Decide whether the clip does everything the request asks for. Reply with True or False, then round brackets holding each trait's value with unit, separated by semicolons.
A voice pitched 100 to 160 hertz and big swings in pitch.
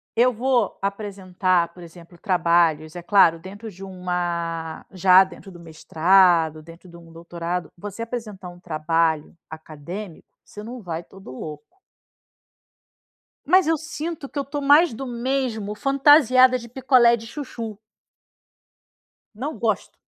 False (190 Hz; 5.9 semitones)